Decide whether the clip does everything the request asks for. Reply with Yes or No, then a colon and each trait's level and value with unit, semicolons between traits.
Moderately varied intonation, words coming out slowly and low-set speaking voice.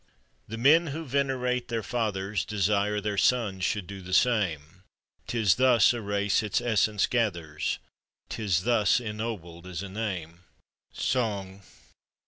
Yes: average, 3.9 semitones; slow, 130 wpm; low, 105 Hz